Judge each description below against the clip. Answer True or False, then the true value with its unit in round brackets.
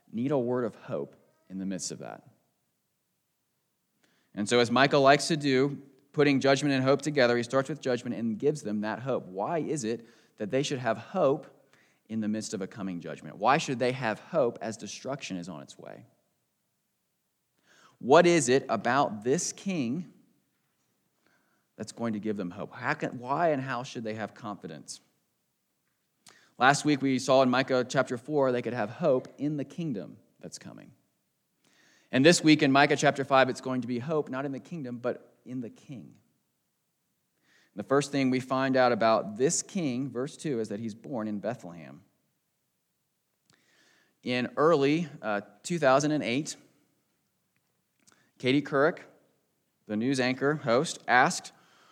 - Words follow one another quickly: False (165 wpm)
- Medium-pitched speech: False (130 Hz)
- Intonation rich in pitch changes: False (3.4 semitones)